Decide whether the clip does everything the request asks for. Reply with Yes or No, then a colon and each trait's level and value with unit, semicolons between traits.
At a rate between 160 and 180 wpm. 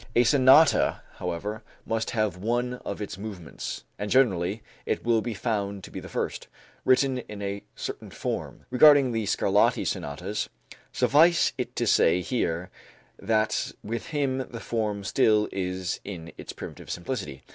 No: average, 150 wpm